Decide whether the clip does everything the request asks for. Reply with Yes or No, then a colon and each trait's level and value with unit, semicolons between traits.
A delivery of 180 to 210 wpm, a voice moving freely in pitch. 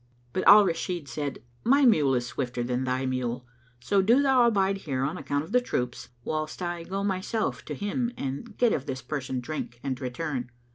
Yes: average, 200 wpm; wide, 7.4 semitones